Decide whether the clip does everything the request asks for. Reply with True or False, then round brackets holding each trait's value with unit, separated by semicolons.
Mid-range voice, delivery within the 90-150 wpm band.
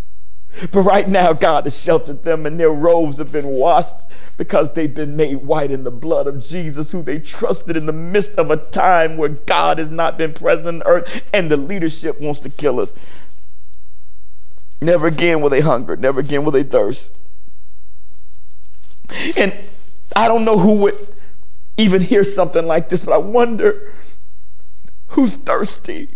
False (155 Hz; 165 wpm)